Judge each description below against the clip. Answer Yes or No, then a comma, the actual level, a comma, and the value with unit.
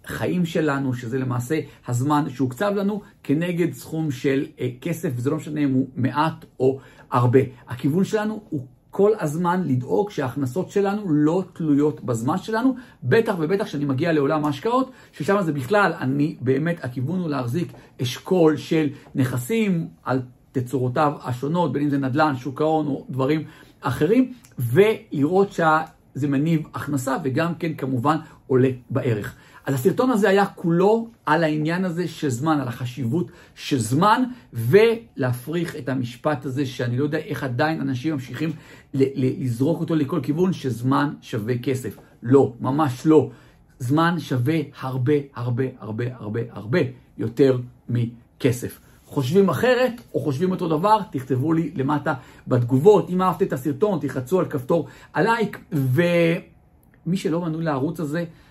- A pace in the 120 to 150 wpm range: Yes, average, 140 wpm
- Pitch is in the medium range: Yes, medium, 150 Hz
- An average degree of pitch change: Yes, average, 4.4 semitones